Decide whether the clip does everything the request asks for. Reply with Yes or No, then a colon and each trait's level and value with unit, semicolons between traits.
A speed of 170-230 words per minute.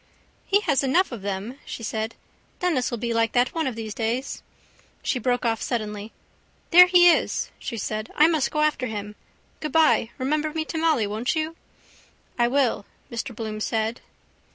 Yes: average, 175 wpm